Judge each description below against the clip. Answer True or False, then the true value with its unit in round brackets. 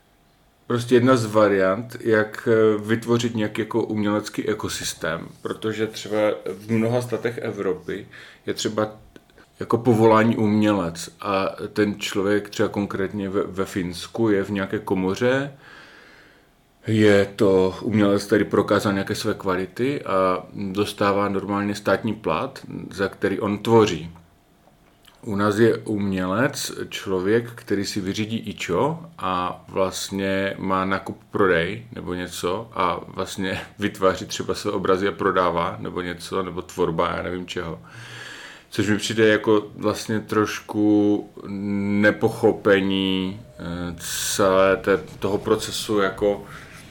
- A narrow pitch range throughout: True (2.3 semitones)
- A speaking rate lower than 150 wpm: True (120 wpm)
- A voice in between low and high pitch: False (100 Hz)